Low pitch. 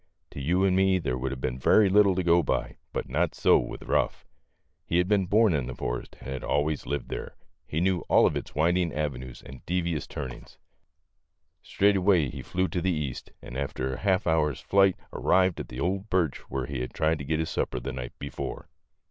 Yes: very low, 80 Hz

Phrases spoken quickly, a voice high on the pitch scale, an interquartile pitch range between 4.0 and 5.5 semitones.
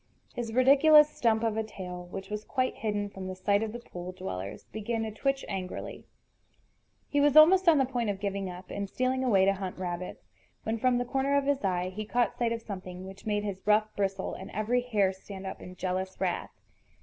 Yes: fast, 215 wpm; high, 210 Hz; average, 4.5 semitones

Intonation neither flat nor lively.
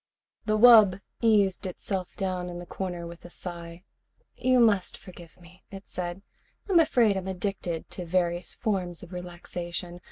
No: narrow, 2.3 semitones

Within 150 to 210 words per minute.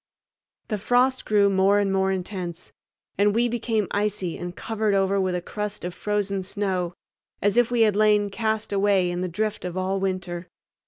Yes: average, 175 wpm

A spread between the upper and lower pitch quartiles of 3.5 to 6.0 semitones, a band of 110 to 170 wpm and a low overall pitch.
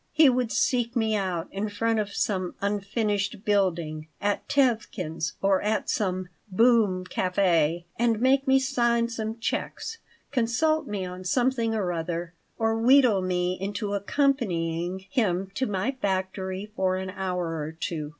No: average, 4.2 semitones; average, 145 wpm; high, 200 Hz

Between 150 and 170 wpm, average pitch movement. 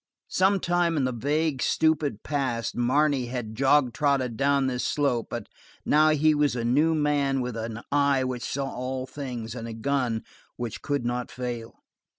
Yes: average, 165 wpm; average, 3.2 semitones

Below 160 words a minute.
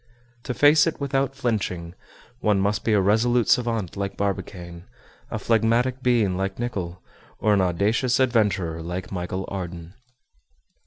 Yes: average, 140 wpm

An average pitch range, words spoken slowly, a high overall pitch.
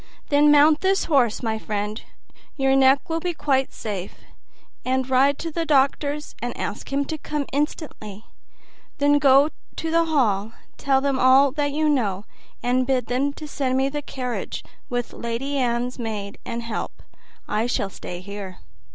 No: average, 3.8 semitones; average, 160 wpm; very high, 265 Hz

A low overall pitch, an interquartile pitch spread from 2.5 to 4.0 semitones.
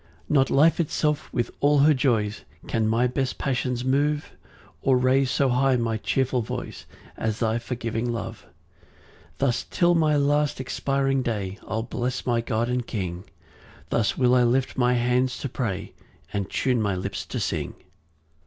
Yes: low, 125 Hz; average, 3.0 semitones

